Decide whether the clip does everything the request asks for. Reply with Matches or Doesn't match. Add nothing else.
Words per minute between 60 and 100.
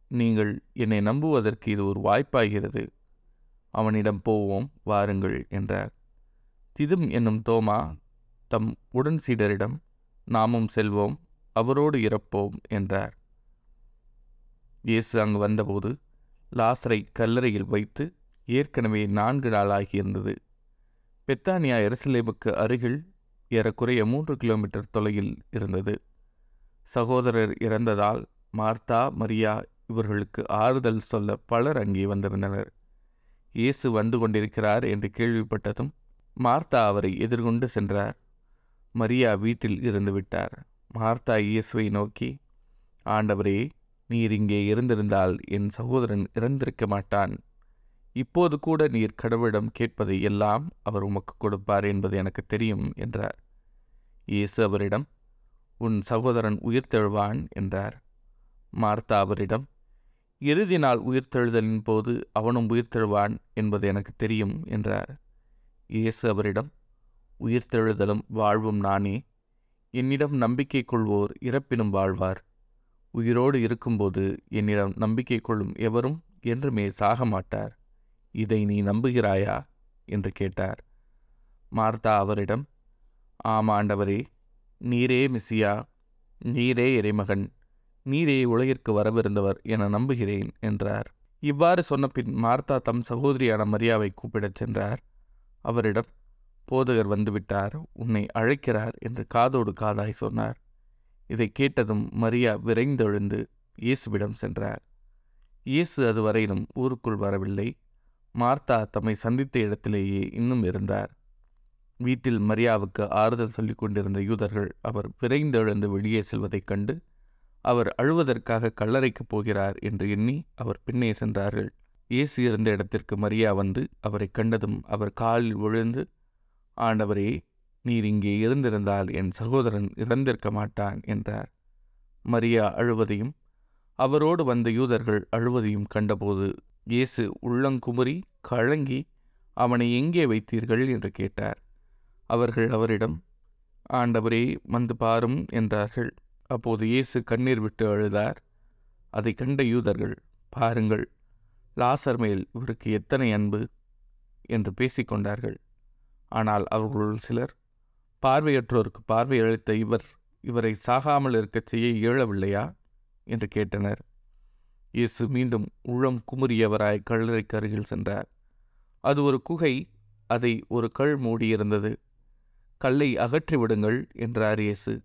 Matches